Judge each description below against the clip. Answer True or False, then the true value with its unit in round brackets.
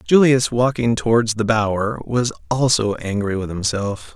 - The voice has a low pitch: True (115 Hz)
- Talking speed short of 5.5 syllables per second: True (4.4 syllables/s)